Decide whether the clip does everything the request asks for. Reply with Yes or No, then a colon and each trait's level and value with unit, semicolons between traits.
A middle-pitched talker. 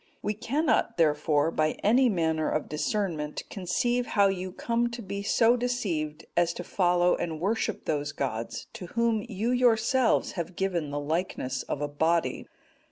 Yes: medium, 180 Hz